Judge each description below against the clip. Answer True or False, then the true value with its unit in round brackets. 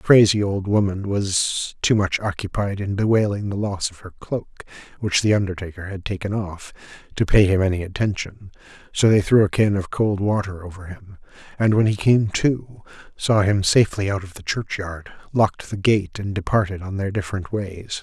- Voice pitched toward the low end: True (100 Hz)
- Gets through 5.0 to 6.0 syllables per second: False (4.7 syllables/s)